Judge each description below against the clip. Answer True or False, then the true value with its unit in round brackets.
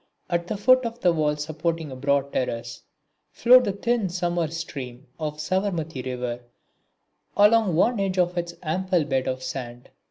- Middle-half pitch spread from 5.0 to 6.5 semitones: True (5.4 semitones)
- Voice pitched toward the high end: False (165 Hz)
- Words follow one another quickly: False (165 wpm)